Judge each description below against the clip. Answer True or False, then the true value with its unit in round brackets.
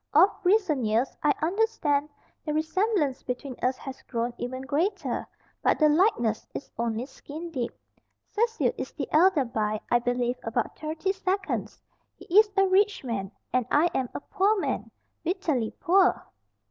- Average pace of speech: True (155 wpm)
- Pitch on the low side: False (300 Hz)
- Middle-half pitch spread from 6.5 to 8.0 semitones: True (7.5 semitones)